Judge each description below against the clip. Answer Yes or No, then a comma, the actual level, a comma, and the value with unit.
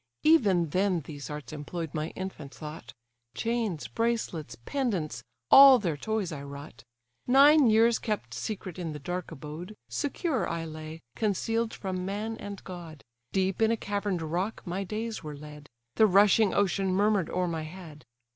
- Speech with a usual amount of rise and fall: No, wide, 5.7 semitones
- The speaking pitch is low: No, medium, 185 Hz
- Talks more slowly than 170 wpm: Yes, average, 155 wpm